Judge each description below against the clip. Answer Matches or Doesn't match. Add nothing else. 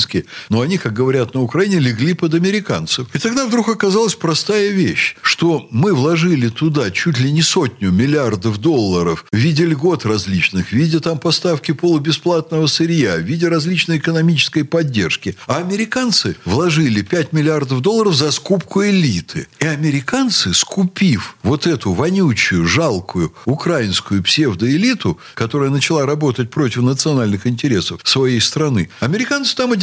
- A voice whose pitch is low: Doesn't match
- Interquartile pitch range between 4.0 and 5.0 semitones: Doesn't match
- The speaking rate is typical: Matches